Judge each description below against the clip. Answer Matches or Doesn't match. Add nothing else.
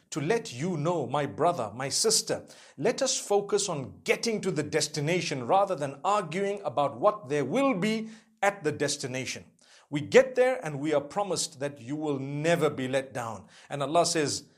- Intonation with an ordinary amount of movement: Doesn't match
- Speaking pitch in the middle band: Matches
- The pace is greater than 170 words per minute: Matches